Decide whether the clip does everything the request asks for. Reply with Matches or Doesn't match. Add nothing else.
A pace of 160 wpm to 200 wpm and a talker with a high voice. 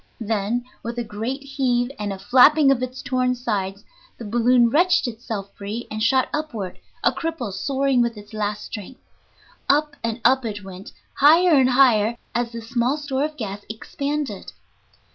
Matches